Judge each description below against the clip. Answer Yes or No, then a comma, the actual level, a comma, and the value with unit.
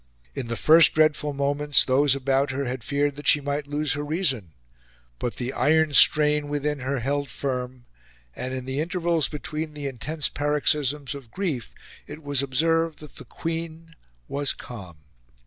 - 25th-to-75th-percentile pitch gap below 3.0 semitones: Yes, narrow, 2.4 semitones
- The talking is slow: No, average, 165 wpm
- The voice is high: No, medium, 145 Hz